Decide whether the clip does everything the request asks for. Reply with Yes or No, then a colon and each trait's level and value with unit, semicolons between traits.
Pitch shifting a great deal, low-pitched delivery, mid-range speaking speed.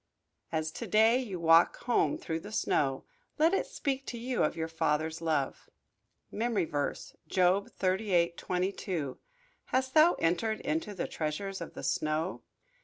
No: wide, 6.1 semitones; medium, 185 Hz; average, 150 wpm